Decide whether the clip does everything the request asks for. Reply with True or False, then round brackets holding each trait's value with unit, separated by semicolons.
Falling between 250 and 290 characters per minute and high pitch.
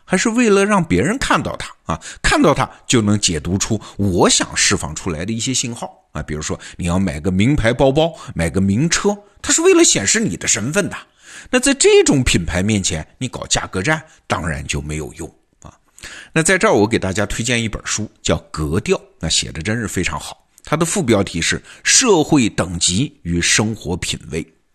False (280 characters per minute; 105 Hz)